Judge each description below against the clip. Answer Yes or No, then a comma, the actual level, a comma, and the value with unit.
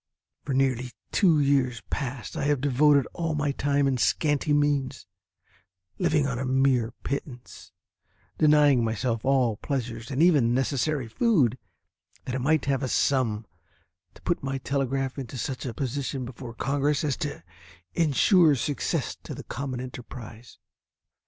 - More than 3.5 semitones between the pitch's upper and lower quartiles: No, narrow, 2.6 semitones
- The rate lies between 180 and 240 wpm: No, average, 145 wpm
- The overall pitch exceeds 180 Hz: No, low, 135 Hz